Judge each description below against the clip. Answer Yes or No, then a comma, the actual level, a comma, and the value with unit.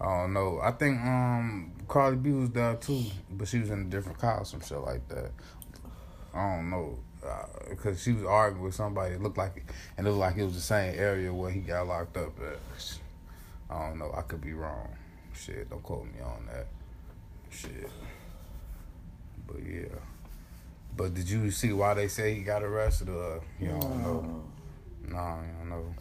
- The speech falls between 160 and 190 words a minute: No, average, 200 wpm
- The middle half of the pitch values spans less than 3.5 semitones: No, average, 3.8 semitones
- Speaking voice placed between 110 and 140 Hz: No, very low, 90 Hz